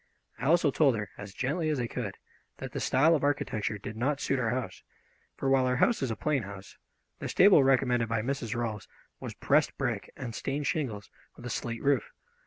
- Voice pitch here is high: No, low, 125 Hz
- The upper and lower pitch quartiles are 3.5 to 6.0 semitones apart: Yes, average, 3.8 semitones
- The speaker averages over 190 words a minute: Yes, fast, 205 wpm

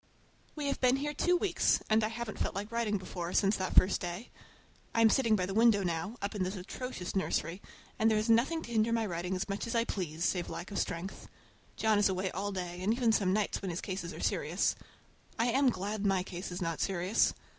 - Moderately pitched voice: No, high, 205 Hz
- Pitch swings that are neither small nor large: Yes, average, 3.9 semitones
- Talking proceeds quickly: Yes, fast, 230 wpm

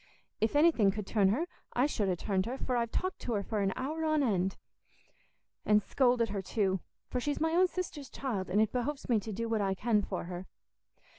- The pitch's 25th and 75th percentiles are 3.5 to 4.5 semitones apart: No, wide, 5.6 semitones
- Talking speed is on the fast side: Yes, fast, 220 wpm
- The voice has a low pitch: No, high, 225 Hz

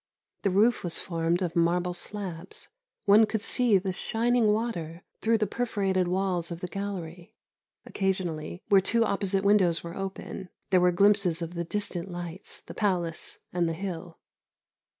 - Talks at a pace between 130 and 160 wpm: Yes, average, 155 wpm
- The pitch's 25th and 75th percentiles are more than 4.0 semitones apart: No, average, 2.9 semitones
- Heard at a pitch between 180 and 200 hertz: Yes, medium, 185 Hz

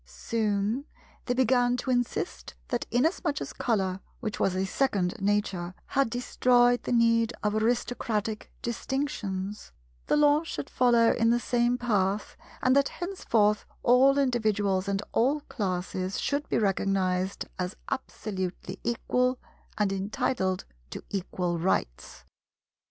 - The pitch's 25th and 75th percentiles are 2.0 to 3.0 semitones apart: No, average, 4.3 semitones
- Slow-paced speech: Yes, slow, 125 wpm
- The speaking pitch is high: Yes, high, 220 Hz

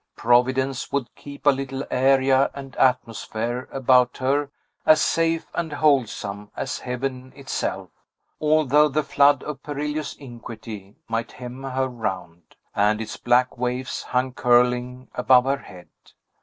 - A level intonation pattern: Yes, narrow, 2.3 semitones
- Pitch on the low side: Yes, low, 130 Hz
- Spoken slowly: Yes, slow, 130 wpm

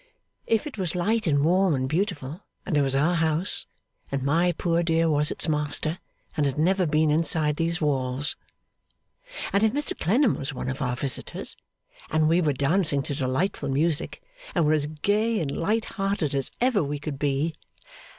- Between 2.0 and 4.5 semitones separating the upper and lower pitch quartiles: Yes, average, 4.1 semitones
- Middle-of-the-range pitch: Yes, medium, 155 Hz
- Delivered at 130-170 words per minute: No, average, 185 wpm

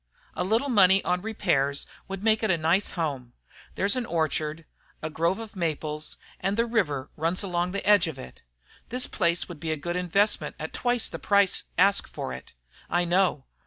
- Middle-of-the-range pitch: Yes, medium, 180 Hz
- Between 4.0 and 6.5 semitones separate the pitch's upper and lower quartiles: Yes, average, 4.3 semitones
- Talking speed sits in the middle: Yes, average, 190 wpm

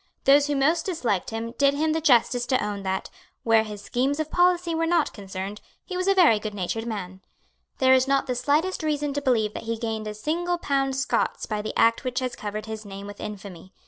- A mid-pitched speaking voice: No, very high, 250 Hz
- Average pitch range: No, wide, 5.7 semitones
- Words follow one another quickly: Yes, fast, 220 wpm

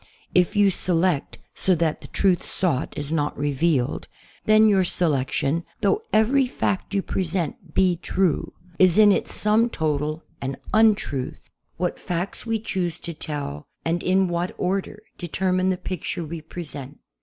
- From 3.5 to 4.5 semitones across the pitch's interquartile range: Yes, average, 3.8 semitones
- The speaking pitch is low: No, medium, 175 Hz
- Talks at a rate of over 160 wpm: No, average, 155 wpm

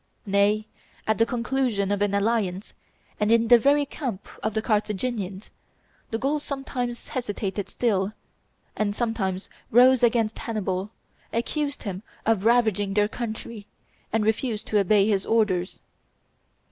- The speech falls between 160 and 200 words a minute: No, slow, 135 wpm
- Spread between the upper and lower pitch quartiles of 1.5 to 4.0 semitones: Yes, average, 2.9 semitones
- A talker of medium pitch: No, high, 220 Hz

